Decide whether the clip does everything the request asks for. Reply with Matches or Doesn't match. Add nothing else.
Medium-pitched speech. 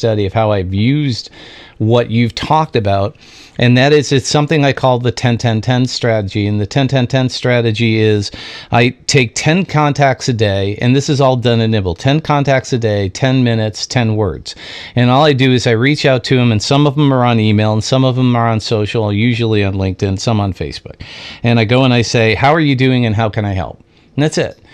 Doesn't match